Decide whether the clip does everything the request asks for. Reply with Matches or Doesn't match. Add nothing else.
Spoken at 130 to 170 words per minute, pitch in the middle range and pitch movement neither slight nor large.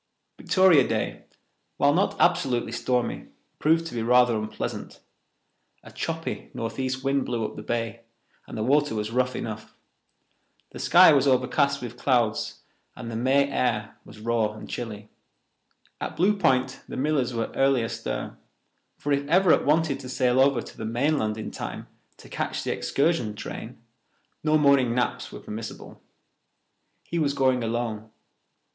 Doesn't match